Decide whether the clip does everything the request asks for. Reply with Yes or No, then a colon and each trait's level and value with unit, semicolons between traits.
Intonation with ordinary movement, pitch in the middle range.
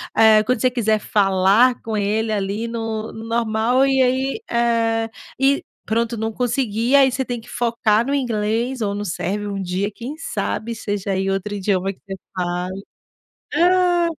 No: average, 3.3 semitones; high, 225 Hz